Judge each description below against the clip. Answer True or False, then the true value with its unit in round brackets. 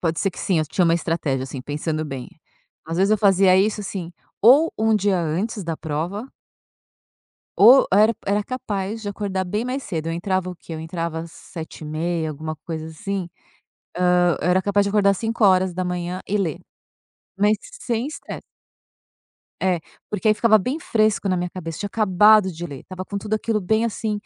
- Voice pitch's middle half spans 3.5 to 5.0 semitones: True (4.0 semitones)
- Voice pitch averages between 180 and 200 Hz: True (190 Hz)